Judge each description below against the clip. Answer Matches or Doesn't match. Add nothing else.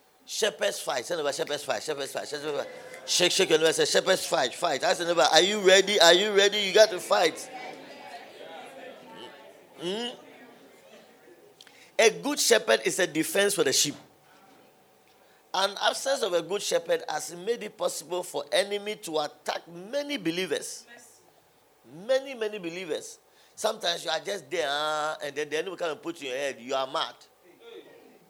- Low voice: Doesn't match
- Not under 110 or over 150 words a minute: Matches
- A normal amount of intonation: Doesn't match